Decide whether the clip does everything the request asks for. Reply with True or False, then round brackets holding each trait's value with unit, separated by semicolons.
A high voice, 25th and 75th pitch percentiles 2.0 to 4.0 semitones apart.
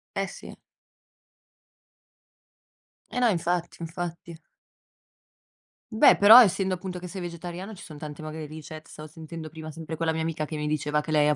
False (165 Hz; 2.5 semitones)